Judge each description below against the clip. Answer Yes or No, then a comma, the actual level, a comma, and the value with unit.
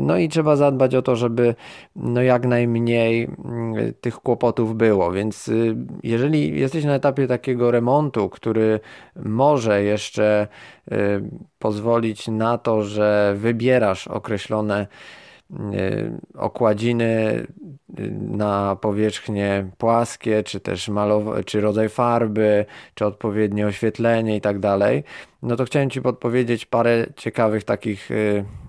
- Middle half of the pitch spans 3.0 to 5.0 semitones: No, narrow, 2.4 semitones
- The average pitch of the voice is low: Yes, low, 110 Hz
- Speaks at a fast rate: No, slow, 110 wpm